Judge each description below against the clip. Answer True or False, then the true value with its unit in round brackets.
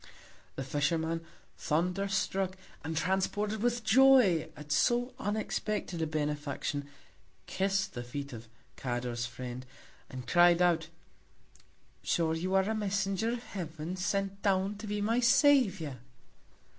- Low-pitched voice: False (185 Hz)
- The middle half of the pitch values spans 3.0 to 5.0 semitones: False (5.5 semitones)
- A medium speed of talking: False (125 wpm)